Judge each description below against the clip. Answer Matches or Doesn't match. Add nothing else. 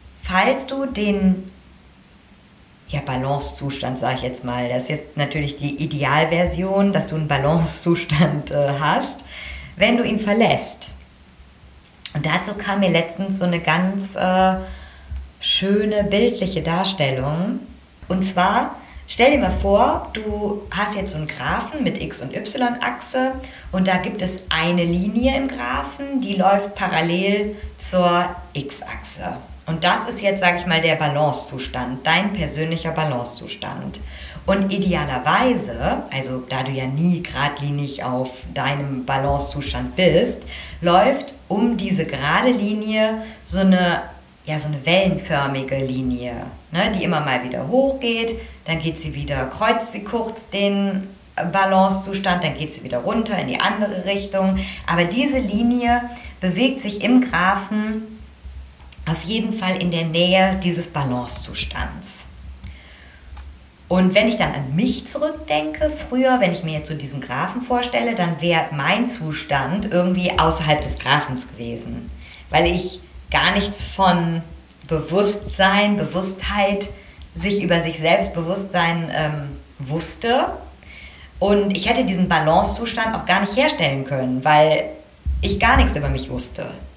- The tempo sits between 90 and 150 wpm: Matches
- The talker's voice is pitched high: Doesn't match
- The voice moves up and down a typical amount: Doesn't match